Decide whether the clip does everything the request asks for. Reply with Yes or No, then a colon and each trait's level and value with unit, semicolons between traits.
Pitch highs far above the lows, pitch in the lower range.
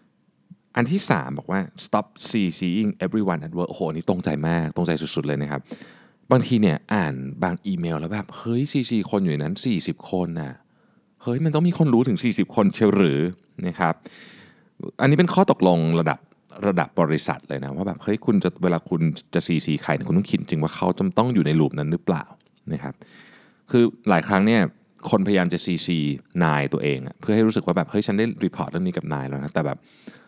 Yes: wide, 6.6 semitones; very low, 90 Hz